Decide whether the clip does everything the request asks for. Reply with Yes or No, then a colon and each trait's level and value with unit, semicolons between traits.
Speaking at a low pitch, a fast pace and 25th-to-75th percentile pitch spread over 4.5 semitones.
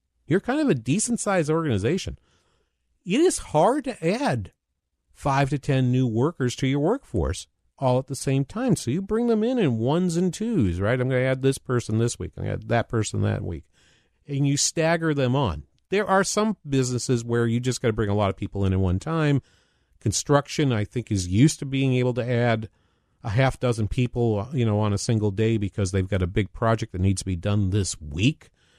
Yes: low, 125 Hz; fast, 225 wpm; wide, 5.6 semitones